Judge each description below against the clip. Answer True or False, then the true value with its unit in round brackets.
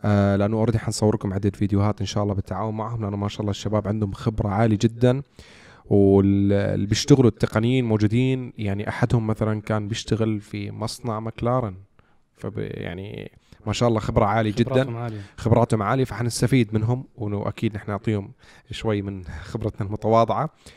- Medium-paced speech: False (145 wpm)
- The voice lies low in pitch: True (110 Hz)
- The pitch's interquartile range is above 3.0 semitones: False (2.4 semitones)